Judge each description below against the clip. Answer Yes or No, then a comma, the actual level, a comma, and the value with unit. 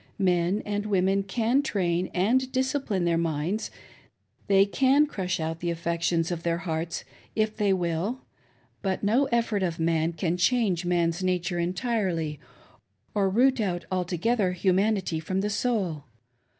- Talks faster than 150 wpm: No, average, 140 wpm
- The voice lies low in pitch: No, medium, 185 Hz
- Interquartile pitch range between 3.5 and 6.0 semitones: Yes, average, 4.0 semitones